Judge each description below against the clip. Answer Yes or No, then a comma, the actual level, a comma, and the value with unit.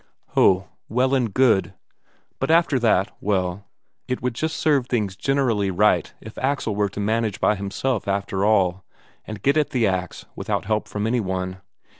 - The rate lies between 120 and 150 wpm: No, average, 170 wpm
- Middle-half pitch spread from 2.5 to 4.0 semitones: No, average, 4.6 semitones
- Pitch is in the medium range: No, low, 105 Hz